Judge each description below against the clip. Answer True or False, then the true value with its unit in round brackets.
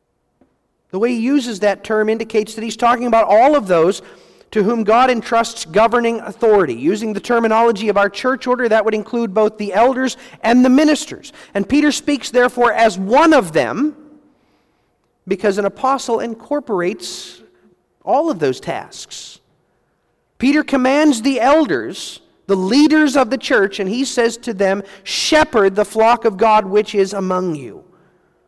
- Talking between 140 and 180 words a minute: True (160 wpm)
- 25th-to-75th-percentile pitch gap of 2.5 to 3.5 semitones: False (3.9 semitones)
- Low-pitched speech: False (230 Hz)